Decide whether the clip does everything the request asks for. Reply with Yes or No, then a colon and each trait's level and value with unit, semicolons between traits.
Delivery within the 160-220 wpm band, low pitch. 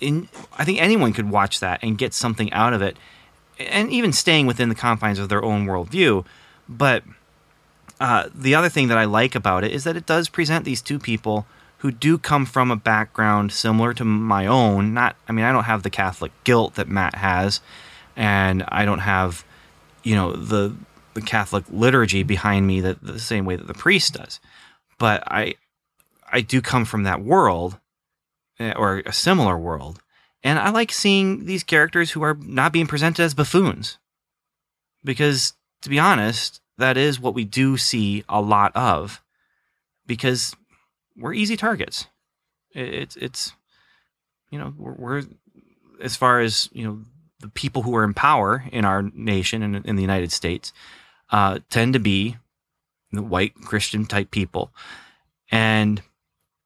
Yes: average, 170 wpm; low, 110 Hz